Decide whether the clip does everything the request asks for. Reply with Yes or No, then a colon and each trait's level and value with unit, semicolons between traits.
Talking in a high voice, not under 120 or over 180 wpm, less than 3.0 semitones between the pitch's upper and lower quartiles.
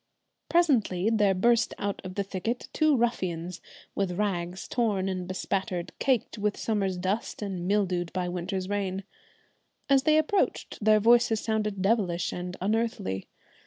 No: high, 200 Hz; average, 140 wpm; average, 3.5 semitones